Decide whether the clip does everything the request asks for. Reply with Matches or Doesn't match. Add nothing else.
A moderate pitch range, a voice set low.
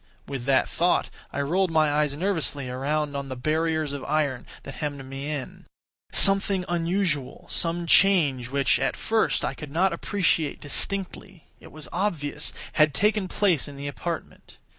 Doesn't match